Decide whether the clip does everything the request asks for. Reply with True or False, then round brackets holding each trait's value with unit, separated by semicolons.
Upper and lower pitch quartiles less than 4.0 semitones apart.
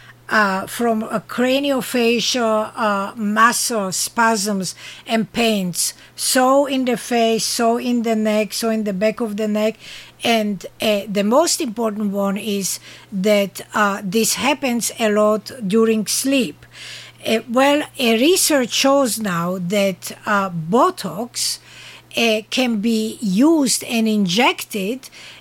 True (2.7 semitones)